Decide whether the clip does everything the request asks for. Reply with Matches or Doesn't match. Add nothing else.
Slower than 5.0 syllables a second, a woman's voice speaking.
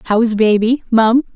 Matches